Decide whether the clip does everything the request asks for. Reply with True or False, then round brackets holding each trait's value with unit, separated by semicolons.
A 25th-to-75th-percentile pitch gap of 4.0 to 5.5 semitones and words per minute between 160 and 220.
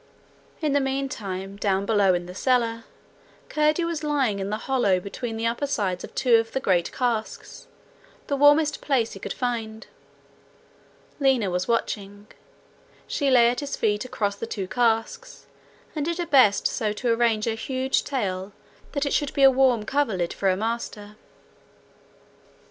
True (4.9 semitones; 165 wpm)